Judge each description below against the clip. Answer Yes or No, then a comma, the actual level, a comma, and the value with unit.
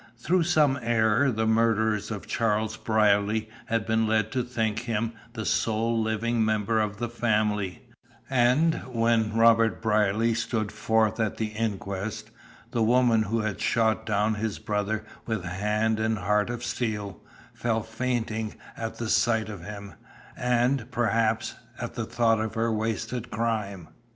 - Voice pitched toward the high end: No, low, 110 Hz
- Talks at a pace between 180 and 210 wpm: No, average, 150 wpm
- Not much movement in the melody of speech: Yes, narrow, 1.4 semitones